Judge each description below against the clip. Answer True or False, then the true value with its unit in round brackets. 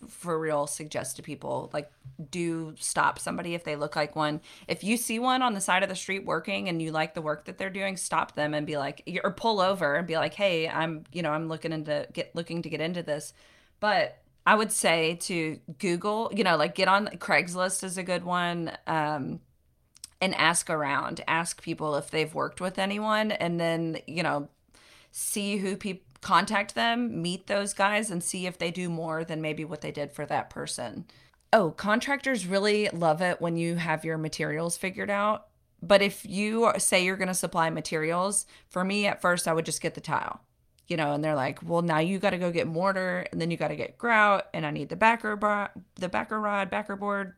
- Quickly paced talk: True (220 wpm)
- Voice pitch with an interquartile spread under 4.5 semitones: True (3.9 semitones)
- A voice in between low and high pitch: True (175 Hz)